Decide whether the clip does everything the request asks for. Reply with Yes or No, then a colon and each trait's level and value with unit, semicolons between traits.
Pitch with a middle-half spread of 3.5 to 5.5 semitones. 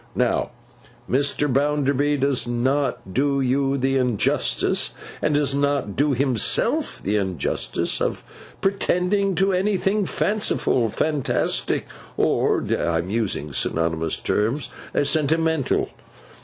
Yes: average, 4.2 semitones